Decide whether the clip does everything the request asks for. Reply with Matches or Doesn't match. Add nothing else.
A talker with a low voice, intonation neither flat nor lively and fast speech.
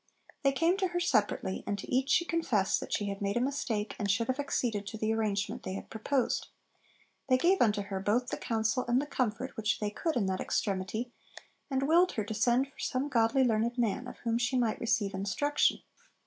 Doesn't match